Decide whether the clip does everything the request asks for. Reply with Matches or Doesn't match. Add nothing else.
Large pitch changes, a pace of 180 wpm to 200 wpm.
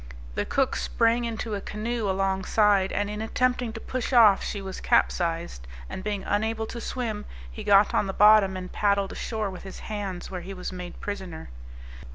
Doesn't match